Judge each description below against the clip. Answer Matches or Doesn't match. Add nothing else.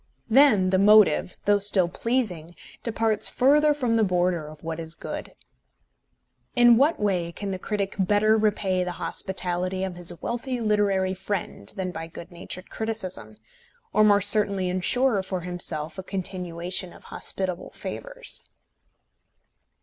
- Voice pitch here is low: Doesn't match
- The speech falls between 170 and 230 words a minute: Doesn't match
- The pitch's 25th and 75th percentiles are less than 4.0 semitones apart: Matches